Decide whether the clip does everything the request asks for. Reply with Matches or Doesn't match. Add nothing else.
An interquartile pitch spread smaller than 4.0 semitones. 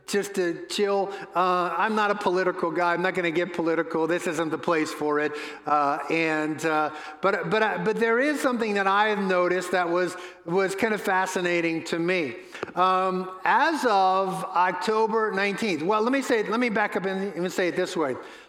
Matches